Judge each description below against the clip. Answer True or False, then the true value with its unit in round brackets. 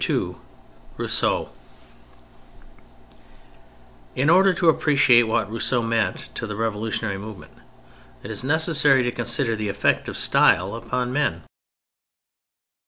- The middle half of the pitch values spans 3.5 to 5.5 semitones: True (4.2 semitones)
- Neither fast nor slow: False (110 wpm)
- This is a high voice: False (115 Hz)